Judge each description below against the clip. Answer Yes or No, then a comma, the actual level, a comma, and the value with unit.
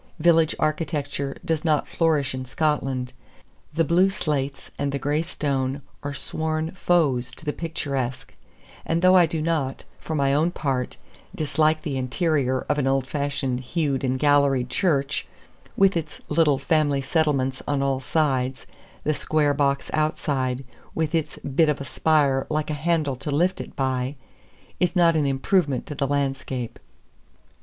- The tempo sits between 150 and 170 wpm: Yes, average, 155 wpm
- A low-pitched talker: No, medium, 145 Hz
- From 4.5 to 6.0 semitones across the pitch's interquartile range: No, average, 2.8 semitones